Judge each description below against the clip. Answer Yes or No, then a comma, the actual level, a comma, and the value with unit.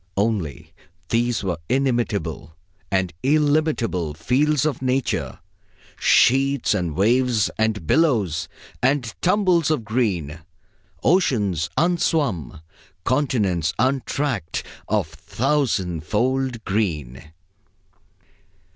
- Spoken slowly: Yes, slow, 85 wpm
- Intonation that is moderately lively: No, wide, 7.5 semitones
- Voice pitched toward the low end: Yes, low, 115 Hz